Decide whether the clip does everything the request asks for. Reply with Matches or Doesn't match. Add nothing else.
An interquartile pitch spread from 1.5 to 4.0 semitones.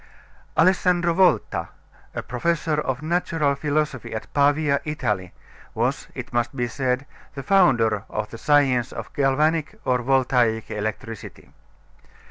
Doesn't match